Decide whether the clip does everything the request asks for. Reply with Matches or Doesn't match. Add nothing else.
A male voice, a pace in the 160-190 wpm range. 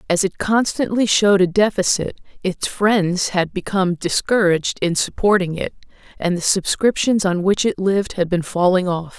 Doesn't match